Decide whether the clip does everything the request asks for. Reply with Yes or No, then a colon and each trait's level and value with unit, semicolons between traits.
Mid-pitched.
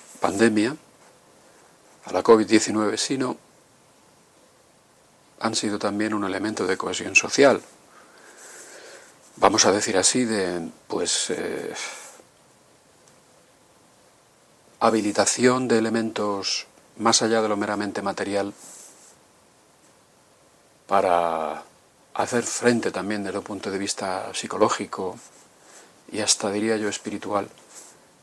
No: low, 105 Hz